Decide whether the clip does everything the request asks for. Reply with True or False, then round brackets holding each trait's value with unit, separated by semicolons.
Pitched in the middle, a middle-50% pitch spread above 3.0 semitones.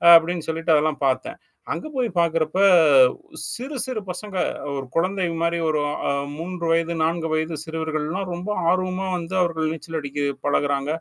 False (165 Hz; 2.7 semitones)